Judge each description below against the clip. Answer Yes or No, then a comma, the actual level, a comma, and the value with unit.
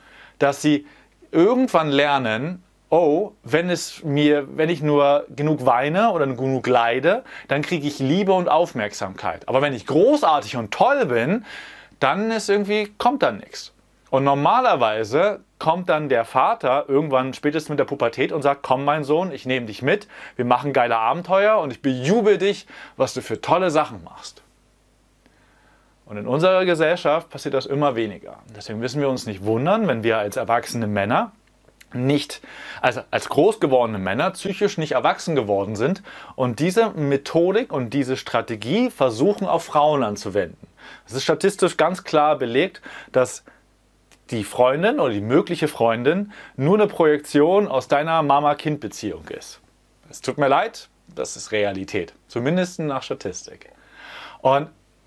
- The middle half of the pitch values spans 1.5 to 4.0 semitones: No, wide, 5.4 semitones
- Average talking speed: Yes, average, 155 wpm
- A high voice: No, medium, 145 Hz